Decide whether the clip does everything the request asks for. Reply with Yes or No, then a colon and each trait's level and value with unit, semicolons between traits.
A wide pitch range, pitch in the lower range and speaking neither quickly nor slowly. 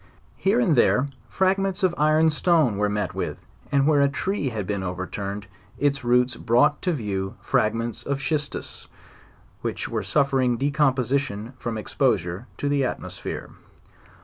Yes: wide, 5.7 semitones; low, 130 Hz; average, 150 wpm